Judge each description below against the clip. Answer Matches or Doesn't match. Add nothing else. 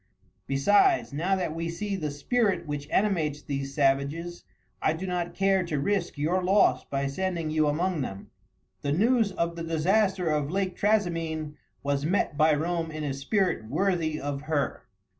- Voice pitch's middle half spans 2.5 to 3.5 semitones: Doesn't match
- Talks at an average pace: Matches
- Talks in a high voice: Doesn't match